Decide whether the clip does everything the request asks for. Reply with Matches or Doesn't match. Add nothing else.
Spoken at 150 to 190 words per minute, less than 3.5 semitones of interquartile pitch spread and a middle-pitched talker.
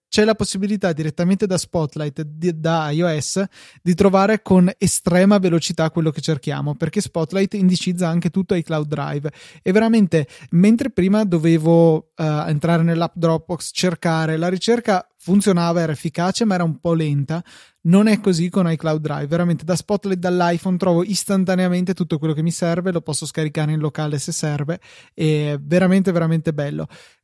Matches